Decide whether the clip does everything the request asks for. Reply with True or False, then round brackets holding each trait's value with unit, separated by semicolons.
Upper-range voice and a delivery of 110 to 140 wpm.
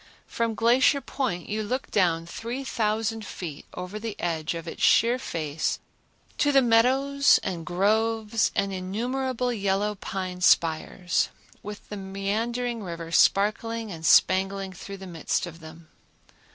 True (205 Hz; 135 wpm)